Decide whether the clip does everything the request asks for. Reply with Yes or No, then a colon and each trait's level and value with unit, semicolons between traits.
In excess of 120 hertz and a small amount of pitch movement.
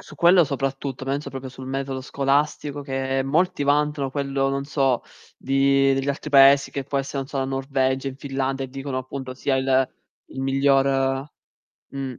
Yes: low, 135 Hz; narrow, 0.8 semitones